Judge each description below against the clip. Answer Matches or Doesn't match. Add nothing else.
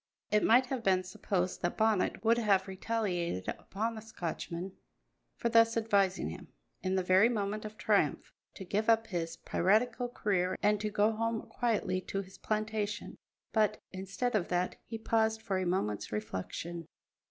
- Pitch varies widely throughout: Doesn't match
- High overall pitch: Matches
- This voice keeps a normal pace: Matches